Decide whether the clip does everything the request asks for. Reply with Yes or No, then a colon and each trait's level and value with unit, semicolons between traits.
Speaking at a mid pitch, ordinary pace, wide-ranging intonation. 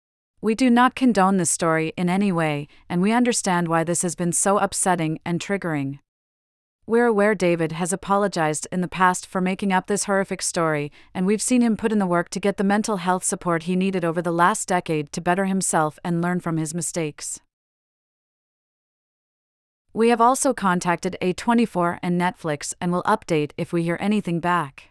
No: medium, 180 Hz; average, 185 wpm; average, 3.1 semitones